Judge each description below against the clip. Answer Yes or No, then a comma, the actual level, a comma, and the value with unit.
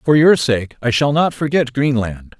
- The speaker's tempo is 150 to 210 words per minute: Yes, average, 200 wpm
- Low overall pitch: Yes, low, 130 Hz